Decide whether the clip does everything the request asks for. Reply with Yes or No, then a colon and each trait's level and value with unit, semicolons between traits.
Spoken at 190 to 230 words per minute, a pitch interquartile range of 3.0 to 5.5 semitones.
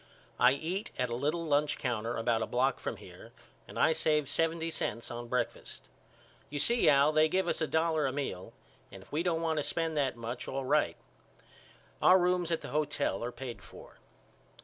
Yes: average, 195 wpm; average, 4.7 semitones